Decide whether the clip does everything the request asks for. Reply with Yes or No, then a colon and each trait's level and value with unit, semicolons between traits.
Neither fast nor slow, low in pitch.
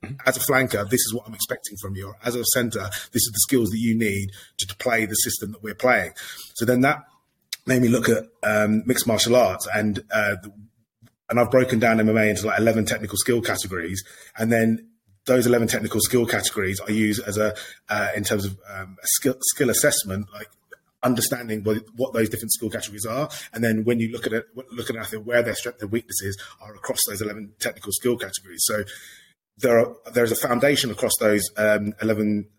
No: fast, 210 wpm; low, 110 Hz